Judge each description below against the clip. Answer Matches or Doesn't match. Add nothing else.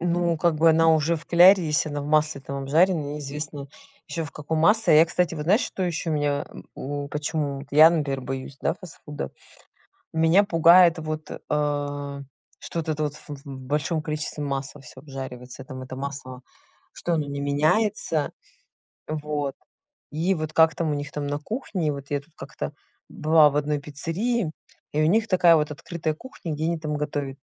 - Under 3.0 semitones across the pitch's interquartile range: Matches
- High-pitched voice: Doesn't match